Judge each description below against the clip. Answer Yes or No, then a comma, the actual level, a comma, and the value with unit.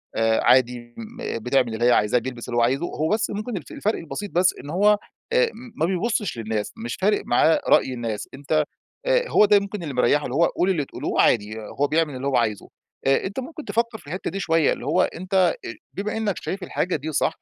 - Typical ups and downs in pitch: No, wide, 8.4 semitones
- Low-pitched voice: No, medium, 155 Hz